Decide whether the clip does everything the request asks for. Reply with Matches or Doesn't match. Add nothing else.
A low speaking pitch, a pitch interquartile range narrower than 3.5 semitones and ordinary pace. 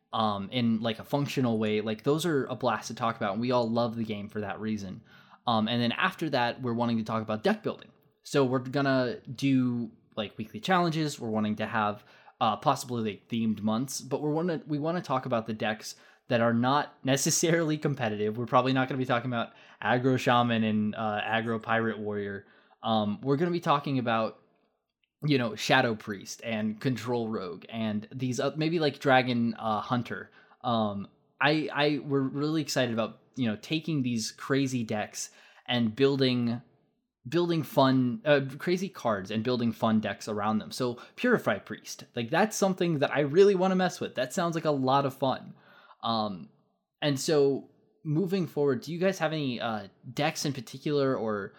Doesn't match